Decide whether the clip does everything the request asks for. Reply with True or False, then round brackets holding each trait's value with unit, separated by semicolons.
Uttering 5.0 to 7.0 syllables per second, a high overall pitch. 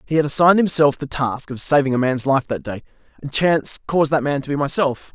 False (6.1 syllables/s; 140 Hz)